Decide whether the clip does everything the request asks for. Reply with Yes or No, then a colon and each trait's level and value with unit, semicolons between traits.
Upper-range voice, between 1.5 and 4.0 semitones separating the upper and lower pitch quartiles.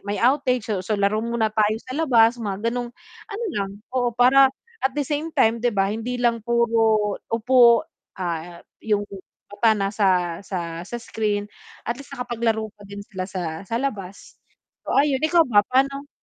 Yes: high, 225 Hz; average, 3.7 semitones